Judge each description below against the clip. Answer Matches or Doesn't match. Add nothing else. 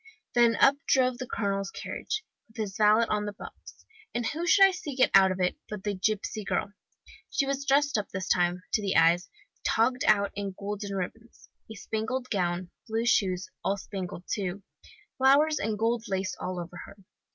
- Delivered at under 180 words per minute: Doesn't match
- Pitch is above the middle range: Matches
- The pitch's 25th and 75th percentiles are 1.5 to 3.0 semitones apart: Doesn't match